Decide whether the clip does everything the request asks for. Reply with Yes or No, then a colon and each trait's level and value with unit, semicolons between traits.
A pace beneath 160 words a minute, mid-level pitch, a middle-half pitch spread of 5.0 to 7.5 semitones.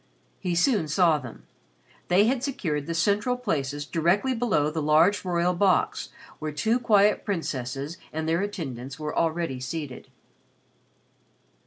Yes: slow, 135 wpm; medium, 170 Hz; average, 5.3 semitones